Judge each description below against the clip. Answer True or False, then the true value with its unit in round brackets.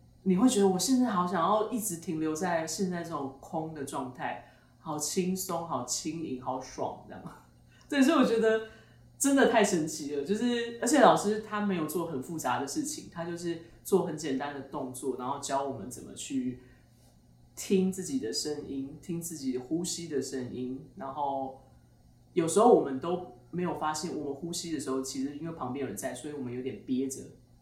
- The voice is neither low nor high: True (160 Hz)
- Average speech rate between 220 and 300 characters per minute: True (280 characters per minute)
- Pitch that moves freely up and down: True (5.7 semitones)